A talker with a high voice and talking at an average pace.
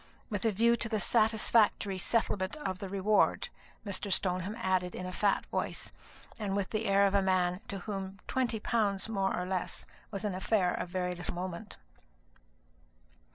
Yes: high, 195 Hz; average, 170 wpm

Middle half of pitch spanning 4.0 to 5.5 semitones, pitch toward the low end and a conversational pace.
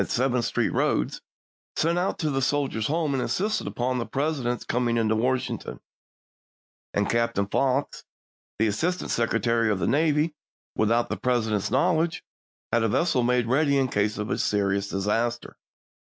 Yes: average, 4.3 semitones; low, 125 Hz; average, 155 wpm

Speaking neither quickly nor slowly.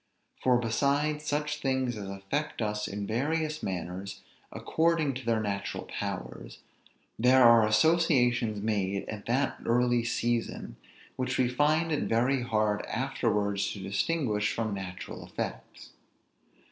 No: slow, 125 wpm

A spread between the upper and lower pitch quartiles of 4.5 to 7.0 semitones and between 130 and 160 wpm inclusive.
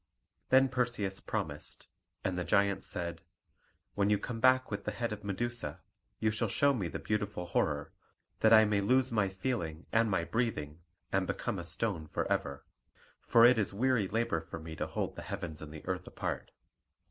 No: average, 4.9 semitones; average, 185 wpm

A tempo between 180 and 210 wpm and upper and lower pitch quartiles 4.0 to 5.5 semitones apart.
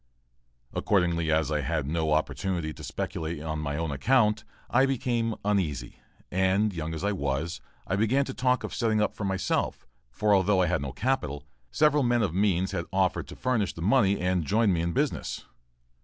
Yes: average, 185 wpm; average, 5.2 semitones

